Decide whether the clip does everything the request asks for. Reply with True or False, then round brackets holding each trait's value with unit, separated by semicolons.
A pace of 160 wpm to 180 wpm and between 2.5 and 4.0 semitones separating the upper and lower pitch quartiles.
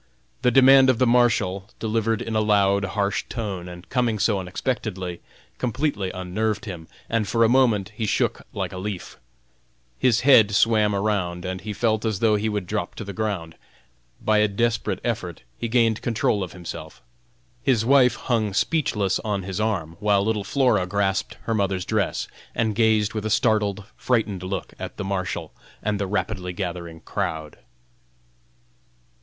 True (165 wpm; 3.1 semitones)